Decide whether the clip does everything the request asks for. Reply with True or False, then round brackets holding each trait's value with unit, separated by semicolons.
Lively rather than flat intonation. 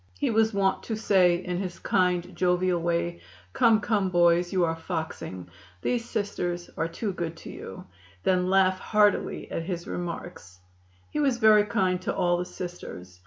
False (2.7 semitones)